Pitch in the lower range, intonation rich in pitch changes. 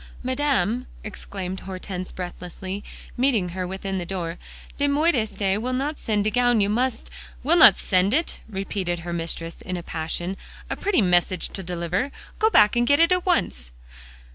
No: high, 195 Hz; wide, 5.9 semitones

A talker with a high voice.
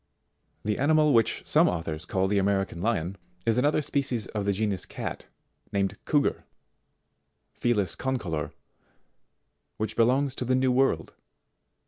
No: low, 110 Hz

